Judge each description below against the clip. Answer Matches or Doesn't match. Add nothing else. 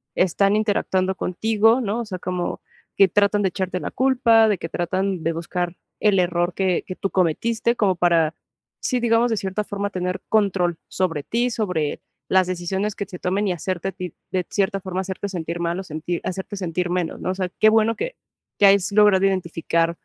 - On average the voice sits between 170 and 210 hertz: Matches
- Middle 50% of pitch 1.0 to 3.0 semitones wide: Matches